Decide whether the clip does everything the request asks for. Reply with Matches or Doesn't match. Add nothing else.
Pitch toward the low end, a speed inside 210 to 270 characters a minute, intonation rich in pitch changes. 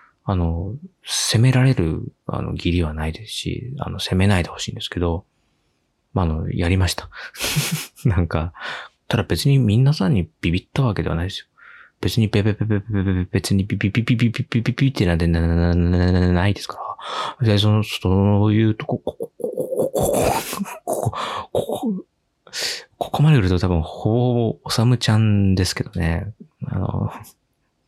Doesn't match